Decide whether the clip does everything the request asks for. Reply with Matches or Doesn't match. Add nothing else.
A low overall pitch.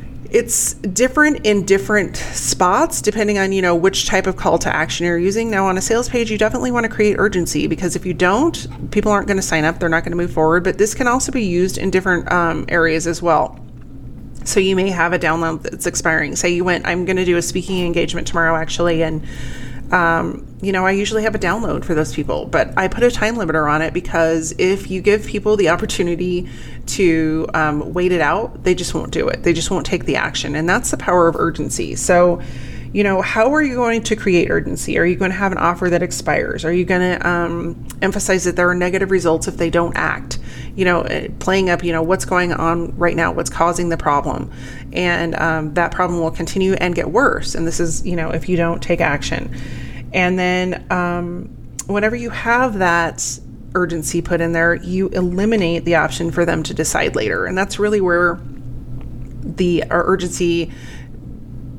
Doesn't match